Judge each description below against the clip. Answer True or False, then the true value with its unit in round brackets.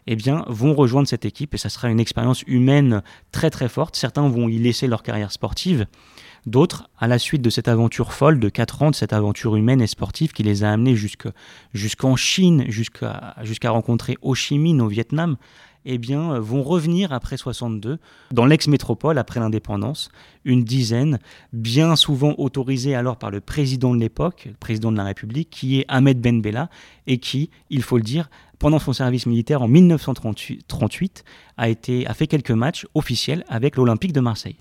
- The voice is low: True (125 Hz)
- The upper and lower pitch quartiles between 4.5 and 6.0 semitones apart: False (3.9 semitones)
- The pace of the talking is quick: False (185 wpm)